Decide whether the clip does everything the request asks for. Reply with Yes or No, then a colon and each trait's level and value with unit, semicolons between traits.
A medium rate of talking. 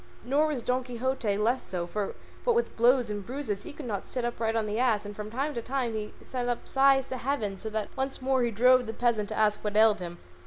No: fast, 250 wpm